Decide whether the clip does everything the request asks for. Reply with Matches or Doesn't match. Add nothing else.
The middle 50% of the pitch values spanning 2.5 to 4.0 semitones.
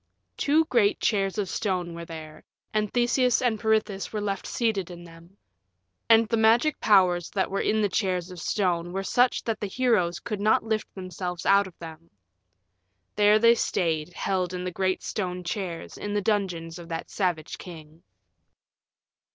Matches